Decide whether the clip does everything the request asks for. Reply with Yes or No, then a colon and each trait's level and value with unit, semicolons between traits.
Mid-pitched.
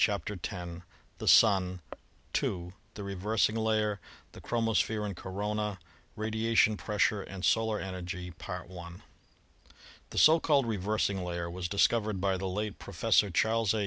No: low, 105 Hz